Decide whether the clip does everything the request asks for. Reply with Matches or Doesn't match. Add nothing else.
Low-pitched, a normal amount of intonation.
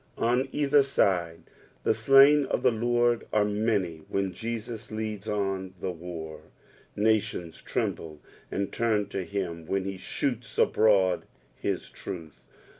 Matches